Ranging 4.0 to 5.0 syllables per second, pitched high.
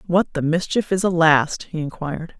No: 4.9 syllables/s; medium, 165 Hz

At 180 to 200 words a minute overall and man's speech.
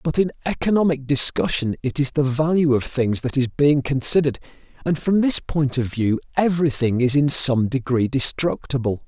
No: average, 170 wpm; male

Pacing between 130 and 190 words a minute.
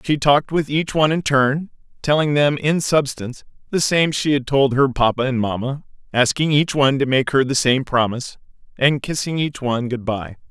No: average, 200 wpm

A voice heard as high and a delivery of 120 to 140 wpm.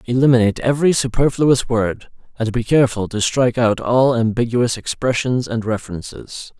No: low, 120 Hz; slow, 135 wpm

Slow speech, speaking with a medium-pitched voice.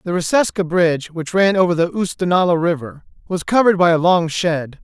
No: average, 185 wpm; medium, 175 Hz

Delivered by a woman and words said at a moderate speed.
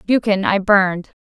Yes: female; average, 145 wpm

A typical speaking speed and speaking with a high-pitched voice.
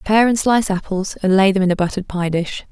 No: fast, 265 wpm; high, 195 Hz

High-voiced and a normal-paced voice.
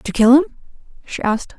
No: high, 240 Hz; fast, 225 wpm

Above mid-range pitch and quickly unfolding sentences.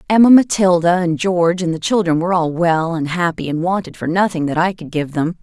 No: medium, 175 Hz; fast, 230 wpm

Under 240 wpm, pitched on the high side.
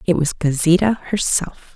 No: slow, 135 wpm; medium, 170 Hz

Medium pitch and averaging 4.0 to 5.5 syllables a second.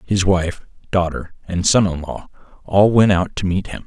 No: very low, 95 Hz; 4.6 syllables/s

